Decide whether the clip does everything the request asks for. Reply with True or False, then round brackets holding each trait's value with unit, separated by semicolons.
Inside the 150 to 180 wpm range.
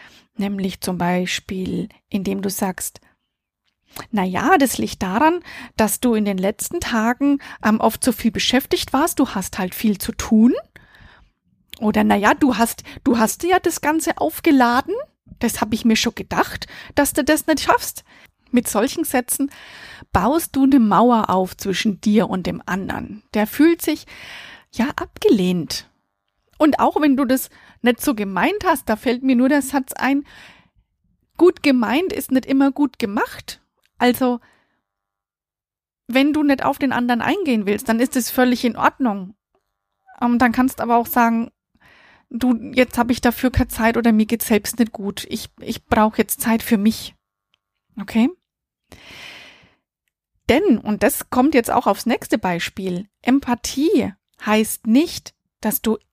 True (160 wpm)